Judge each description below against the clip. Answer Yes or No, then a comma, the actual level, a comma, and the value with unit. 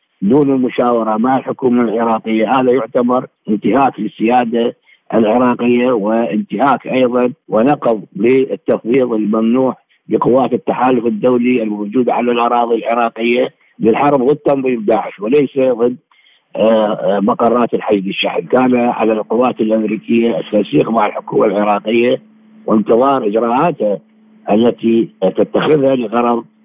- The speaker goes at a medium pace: Yes, average, 100 wpm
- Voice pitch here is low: Yes, low, 120 Hz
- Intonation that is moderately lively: No, narrow, 2.3 semitones